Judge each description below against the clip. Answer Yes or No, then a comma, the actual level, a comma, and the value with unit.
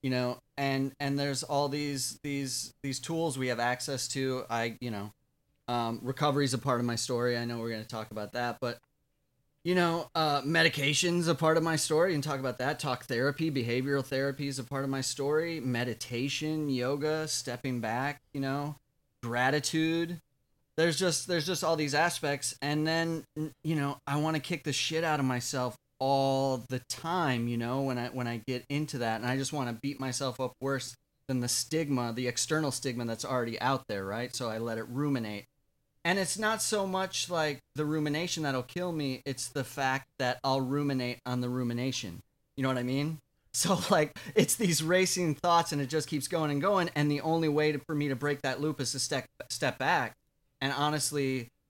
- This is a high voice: No, medium, 140 Hz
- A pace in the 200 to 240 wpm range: Yes, fast, 205 wpm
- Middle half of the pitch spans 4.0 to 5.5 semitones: No, average, 3.4 semitones